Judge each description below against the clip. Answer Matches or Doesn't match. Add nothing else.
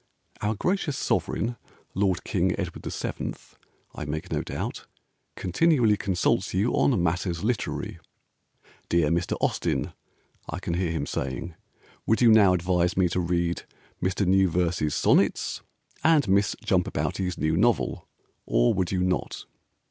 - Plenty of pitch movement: Doesn't match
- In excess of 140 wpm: Doesn't match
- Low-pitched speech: Matches